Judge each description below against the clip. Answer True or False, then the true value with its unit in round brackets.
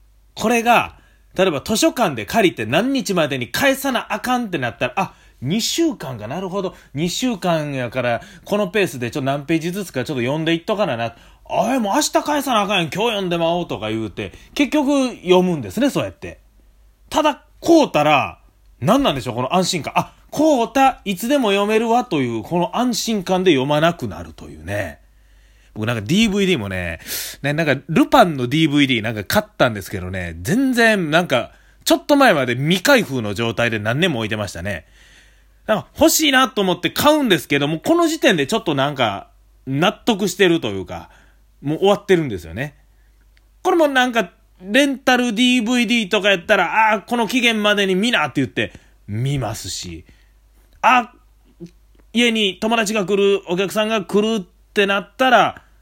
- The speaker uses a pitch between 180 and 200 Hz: True (185 Hz)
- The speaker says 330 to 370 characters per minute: True (360 characters per minute)